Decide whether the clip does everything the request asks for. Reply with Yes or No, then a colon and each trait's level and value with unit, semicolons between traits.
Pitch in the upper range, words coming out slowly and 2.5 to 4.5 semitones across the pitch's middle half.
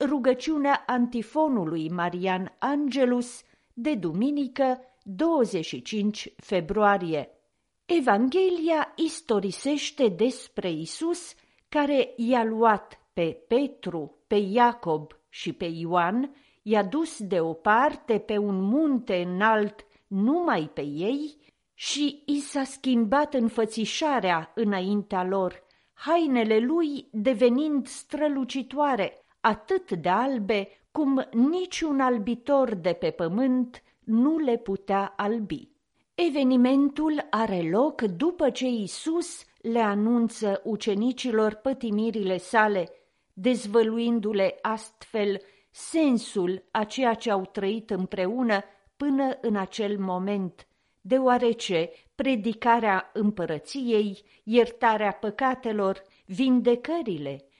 No: high, 230 Hz; slow, 90 wpm; average, 5.3 semitones